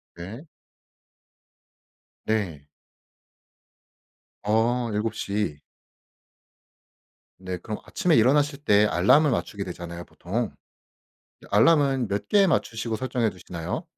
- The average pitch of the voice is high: No, low, 110 Hz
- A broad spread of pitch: Yes, wide, 5.7 semitones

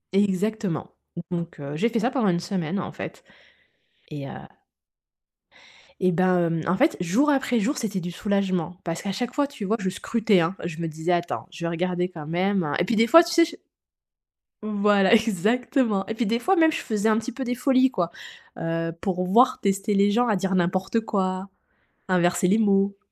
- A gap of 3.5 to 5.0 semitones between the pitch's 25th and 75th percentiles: Yes, average, 4.4 semitones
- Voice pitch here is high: Yes, high, 195 Hz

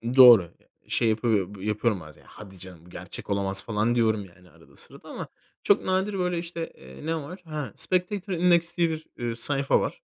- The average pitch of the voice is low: Yes, low, 120 Hz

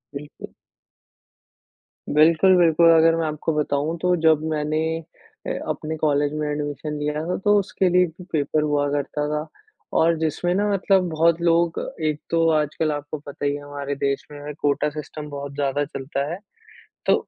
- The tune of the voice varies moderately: No, narrow, 2.2 semitones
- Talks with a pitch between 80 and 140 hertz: No, medium, 150 Hz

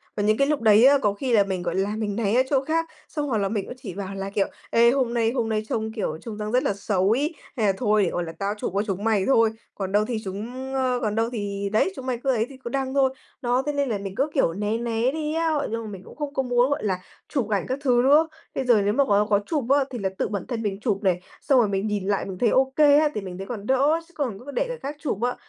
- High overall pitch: Yes, high, 225 Hz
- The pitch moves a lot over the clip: No, average, 4.7 semitones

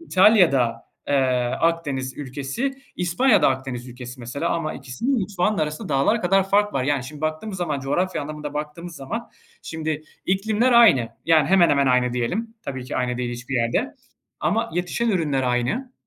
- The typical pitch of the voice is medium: Yes, medium, 155 Hz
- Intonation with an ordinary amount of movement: No, wide, 6.4 semitones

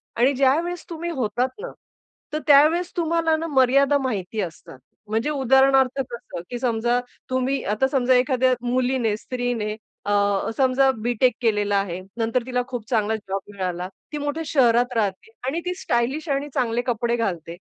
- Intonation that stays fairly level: No, average, 3.7 semitones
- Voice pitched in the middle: No, very high, 250 Hz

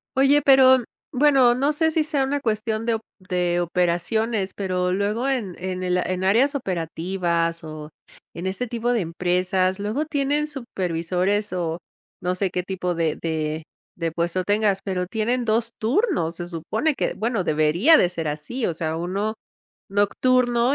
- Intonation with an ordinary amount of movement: No, wide, 5.7 semitones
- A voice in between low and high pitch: No, high, 195 Hz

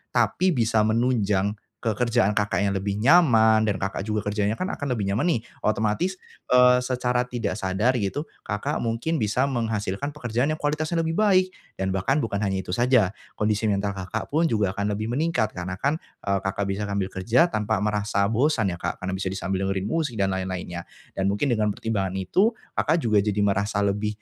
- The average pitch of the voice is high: No, low, 105 Hz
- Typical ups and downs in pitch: Yes, average, 4.2 semitones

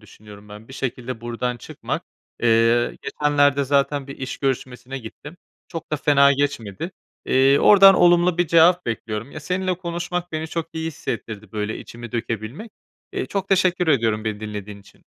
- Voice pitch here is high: No, low, 135 Hz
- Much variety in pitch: Yes, wide, 6.6 semitones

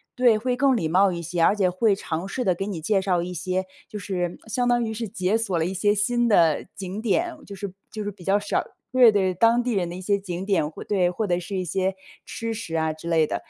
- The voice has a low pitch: No, high, 195 Hz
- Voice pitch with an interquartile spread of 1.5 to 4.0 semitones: Yes, average, 3.6 semitones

